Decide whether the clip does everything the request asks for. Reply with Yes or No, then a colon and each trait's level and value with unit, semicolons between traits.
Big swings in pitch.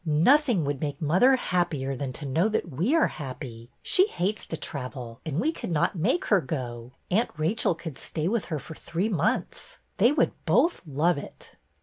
Yes: wide, 7.1 semitones